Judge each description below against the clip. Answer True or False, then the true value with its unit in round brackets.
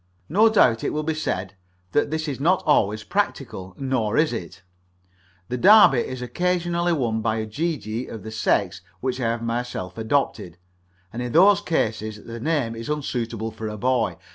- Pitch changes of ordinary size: False (5.7 semitones)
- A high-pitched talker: False (120 Hz)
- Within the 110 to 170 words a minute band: False (180 wpm)